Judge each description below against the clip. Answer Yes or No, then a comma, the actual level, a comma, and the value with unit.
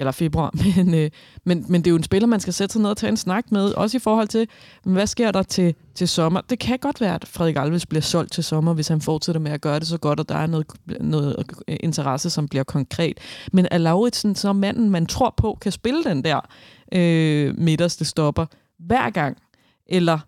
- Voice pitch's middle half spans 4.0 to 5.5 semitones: Yes, average, 4.3 semitones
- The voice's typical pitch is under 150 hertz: No, medium, 170 Hz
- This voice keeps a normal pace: No, fast, 230 wpm